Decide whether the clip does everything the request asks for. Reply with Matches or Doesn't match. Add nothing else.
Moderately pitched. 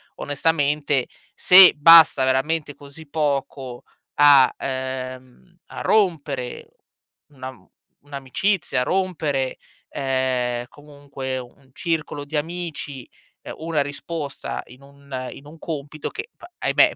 Matches